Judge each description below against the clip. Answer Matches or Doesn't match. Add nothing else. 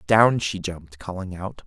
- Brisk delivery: Doesn't match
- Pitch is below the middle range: Matches